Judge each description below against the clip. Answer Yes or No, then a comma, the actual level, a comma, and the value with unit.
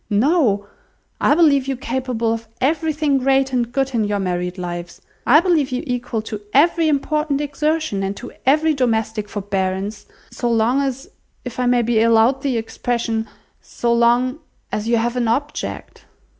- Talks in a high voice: Yes, high, 245 Hz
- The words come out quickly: No, average, 155 wpm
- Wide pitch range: No, average, 3.9 semitones